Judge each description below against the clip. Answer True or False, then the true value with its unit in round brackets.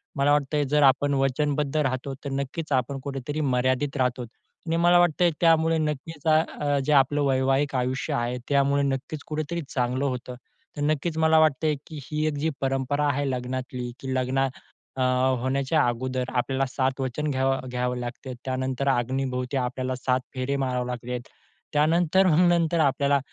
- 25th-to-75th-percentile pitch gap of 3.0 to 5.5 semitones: False (2.6 semitones)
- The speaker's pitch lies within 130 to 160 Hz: True (135 Hz)